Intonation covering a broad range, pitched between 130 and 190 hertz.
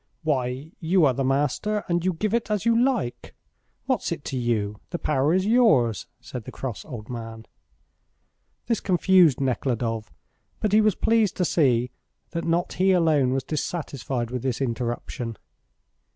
Yes: wide, 7.2 semitones; medium, 140 Hz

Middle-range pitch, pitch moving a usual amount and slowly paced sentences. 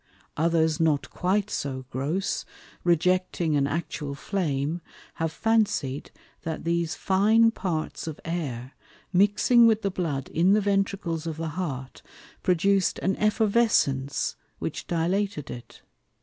Yes: medium, 170 Hz; average, 4.7 semitones; slow, 120 wpm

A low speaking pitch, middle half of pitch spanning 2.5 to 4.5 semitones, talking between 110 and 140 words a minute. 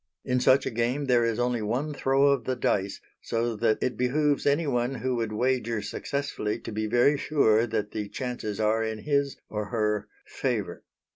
No: low, 120 Hz; average, 3.7 semitones; average, 185 wpm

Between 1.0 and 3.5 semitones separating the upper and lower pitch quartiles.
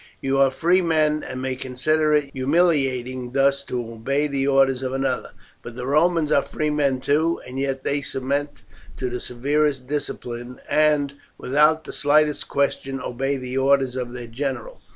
Yes: narrow, 2.6 semitones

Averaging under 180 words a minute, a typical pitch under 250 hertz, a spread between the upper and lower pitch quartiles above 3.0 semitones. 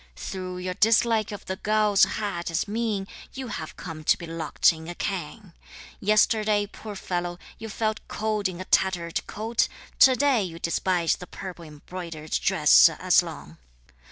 Yes: average, 160 wpm; high, 190 Hz; average, 4.0 semitones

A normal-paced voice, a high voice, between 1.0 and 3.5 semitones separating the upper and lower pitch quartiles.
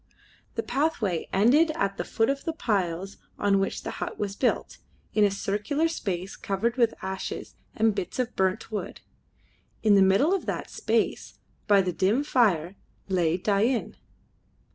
No: average, 160 wpm; high, 205 Hz; average, 4.0 semitones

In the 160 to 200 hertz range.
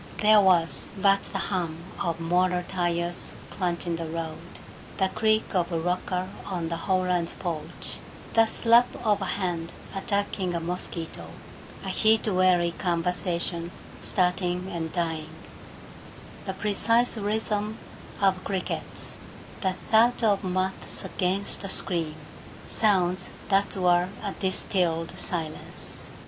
Yes: medium, 185 Hz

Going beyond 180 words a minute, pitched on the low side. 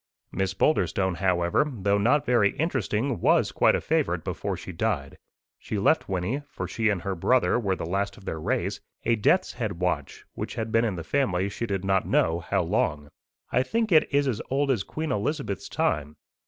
Yes: average, 195 wpm; low, 100 Hz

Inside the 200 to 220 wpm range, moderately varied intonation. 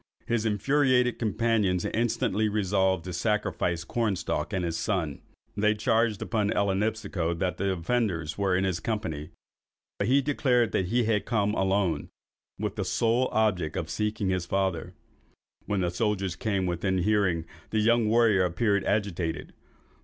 No: average, 150 wpm; average, 3.5 semitones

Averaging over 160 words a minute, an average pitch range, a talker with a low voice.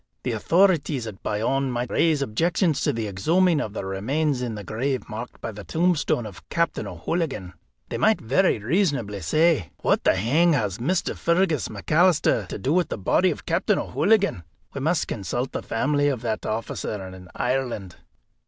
No: average, 170 wpm; wide, 7.3 semitones; low, 130 Hz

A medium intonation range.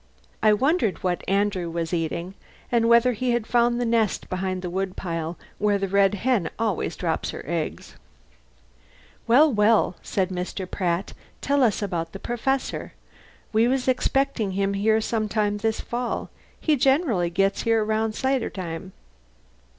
Yes: average, 4.2 semitones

